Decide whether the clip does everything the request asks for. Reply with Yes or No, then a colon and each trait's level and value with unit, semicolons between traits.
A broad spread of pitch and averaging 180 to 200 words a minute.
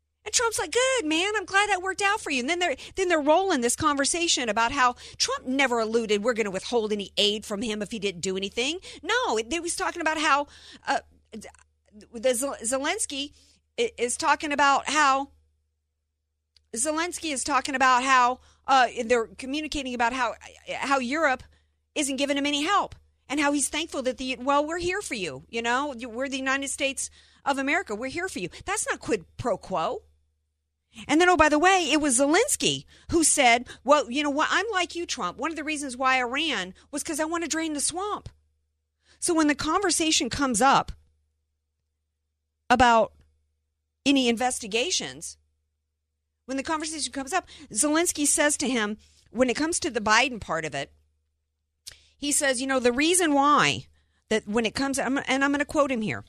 Yes: wide, 6.8 semitones; average, 185 wpm